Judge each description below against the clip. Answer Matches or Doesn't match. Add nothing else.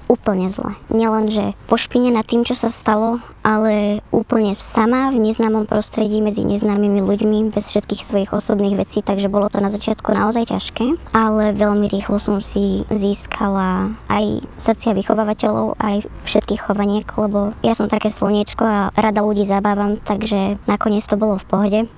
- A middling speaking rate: Matches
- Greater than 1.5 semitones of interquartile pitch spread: Doesn't match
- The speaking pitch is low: Doesn't match